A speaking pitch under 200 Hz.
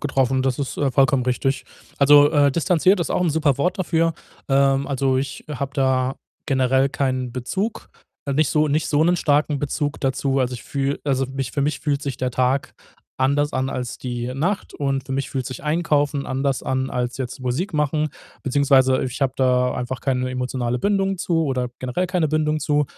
Yes: low, 135 Hz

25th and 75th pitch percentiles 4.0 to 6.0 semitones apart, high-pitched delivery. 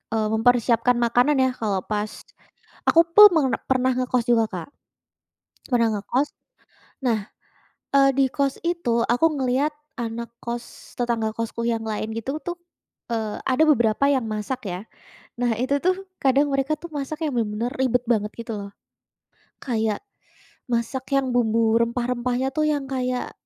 No: average, 3.1 semitones; high, 245 Hz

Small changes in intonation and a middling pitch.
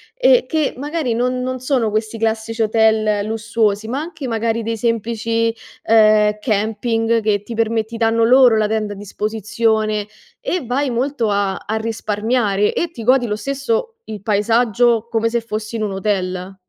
No: narrow, 2.1 semitones; high, 225 Hz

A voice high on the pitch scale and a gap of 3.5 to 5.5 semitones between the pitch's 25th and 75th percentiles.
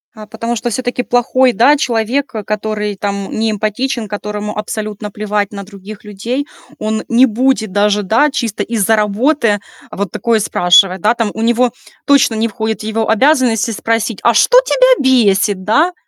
No: high, 220 Hz; average, 2.8 semitones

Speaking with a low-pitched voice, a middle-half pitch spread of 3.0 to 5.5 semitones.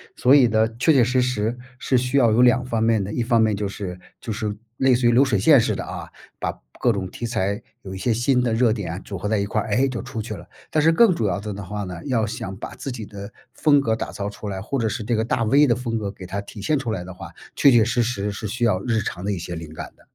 Yes: low, 110 Hz; average, 3.6 semitones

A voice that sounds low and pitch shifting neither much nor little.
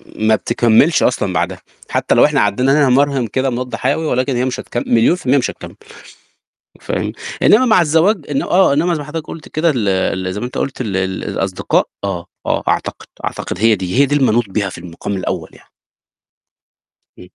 No: low, 125 Hz; wide, 6.2 semitones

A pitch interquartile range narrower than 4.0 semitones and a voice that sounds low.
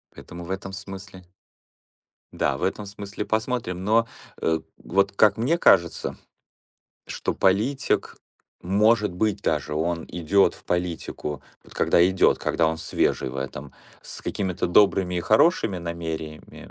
Yes: average, 3.5 semitones; very low, 95 Hz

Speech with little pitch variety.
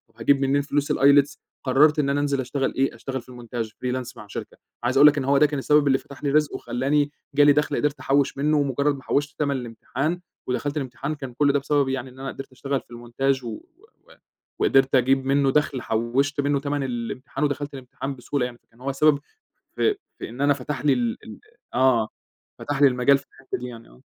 Yes: narrow, 2.1 semitones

